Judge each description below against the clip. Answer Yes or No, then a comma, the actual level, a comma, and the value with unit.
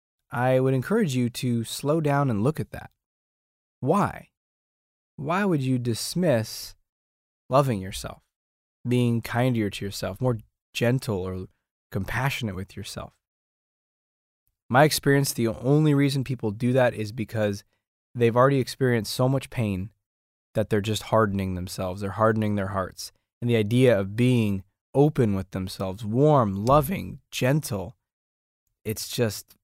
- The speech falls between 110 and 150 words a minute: Yes, slow, 135 wpm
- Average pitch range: Yes, average, 4.5 semitones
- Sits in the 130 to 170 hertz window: No, low, 110 Hz